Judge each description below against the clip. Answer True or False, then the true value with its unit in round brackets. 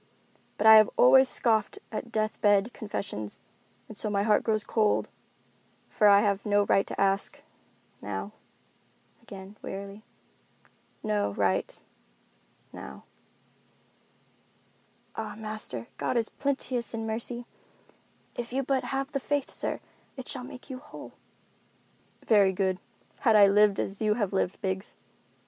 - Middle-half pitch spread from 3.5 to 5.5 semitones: False (3.1 semitones)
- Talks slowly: True (130 wpm)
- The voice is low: False (210 Hz)